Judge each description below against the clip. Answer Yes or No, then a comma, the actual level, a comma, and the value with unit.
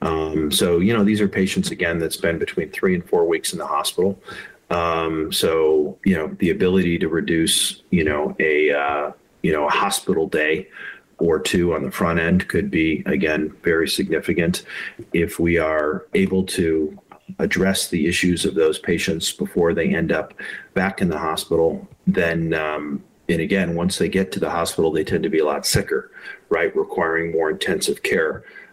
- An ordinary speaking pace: Yes, average, 180 wpm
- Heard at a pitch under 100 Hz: Yes, very low, 90 Hz